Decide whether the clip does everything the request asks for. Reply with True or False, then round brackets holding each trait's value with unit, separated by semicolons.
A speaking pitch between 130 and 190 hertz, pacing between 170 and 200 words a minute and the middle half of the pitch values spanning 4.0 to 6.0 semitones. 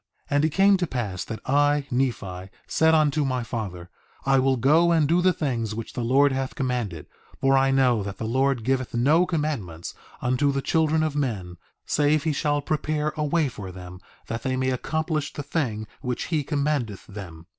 True (135 Hz; 195 wpm; 4.8 semitones)